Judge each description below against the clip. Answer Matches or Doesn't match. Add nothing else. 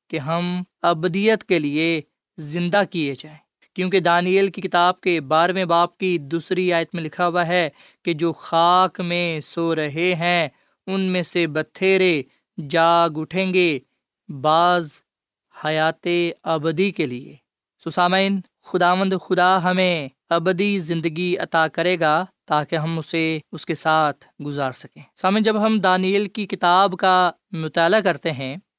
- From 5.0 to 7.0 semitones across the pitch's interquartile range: Doesn't match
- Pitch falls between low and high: Matches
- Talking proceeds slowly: Doesn't match